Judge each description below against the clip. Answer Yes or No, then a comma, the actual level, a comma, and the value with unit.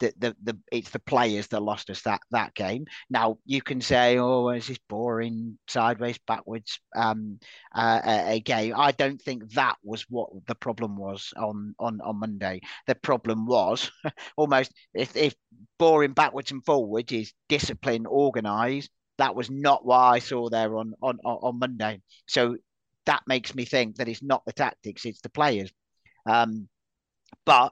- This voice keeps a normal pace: Yes, average, 170 wpm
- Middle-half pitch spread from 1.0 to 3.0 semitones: Yes, average, 2.7 semitones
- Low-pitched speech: Yes, low, 115 Hz